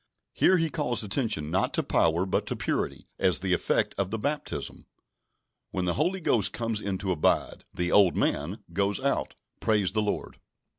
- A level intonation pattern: No, average, 4.0 semitones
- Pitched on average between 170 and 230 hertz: No, low, 100 Hz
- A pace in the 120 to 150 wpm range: No, average, 180 wpm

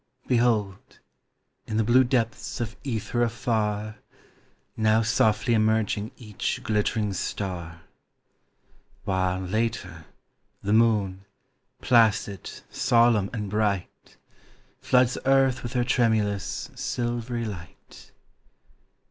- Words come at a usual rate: No, slow, 90 wpm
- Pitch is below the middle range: Yes, low, 110 Hz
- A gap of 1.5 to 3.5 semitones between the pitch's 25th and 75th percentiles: Yes, average, 2.8 semitones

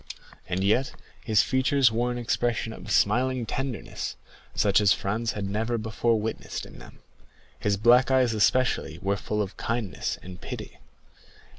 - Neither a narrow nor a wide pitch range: Yes, average, 3.0 semitones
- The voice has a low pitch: Yes, low, 115 Hz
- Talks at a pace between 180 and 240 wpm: No, average, 150 wpm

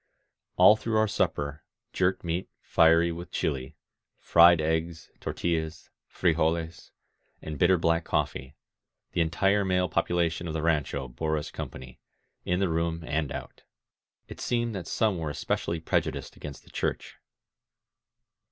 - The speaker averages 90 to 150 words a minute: Yes, average, 145 wpm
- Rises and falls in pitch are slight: Yes, narrow, 2.1 semitones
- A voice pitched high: No, very low, 85 Hz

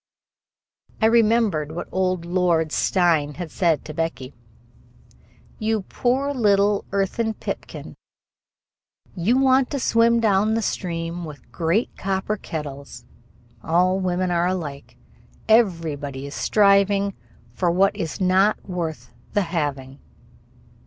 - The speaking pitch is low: No, medium, 185 Hz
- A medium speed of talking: No, slow, 115 wpm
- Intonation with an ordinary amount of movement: Yes, average, 4.4 semitones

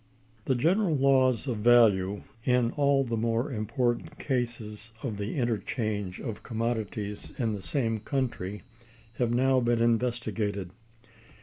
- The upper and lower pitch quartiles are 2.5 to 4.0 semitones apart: Yes, average, 3.2 semitones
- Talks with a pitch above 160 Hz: No, low, 115 Hz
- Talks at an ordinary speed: No, slow, 125 wpm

